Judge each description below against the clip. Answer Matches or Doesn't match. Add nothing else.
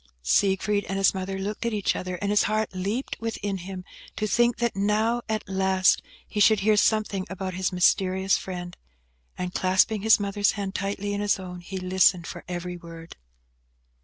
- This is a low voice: Doesn't match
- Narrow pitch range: Matches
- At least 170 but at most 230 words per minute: Matches